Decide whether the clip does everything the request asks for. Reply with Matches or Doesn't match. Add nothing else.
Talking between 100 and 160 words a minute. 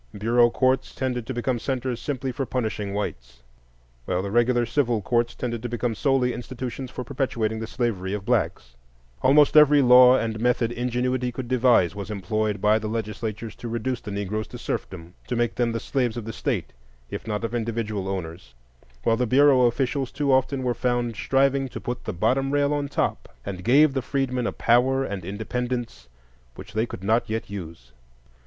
Doesn't match